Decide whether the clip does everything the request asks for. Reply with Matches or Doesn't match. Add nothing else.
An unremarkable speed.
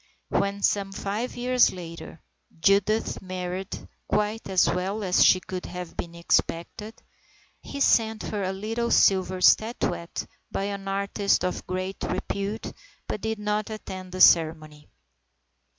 Doesn't match